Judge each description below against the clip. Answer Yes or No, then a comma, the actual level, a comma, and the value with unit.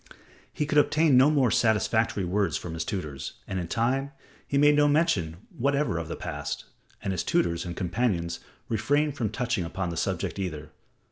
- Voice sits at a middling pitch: No, low, 105 Hz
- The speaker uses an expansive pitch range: Yes, wide, 8.3 semitones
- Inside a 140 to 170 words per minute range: No, average, 180 wpm